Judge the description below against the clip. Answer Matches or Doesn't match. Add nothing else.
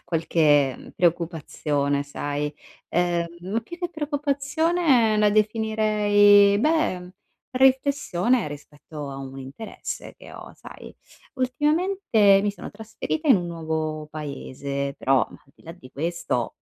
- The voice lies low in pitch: Doesn't match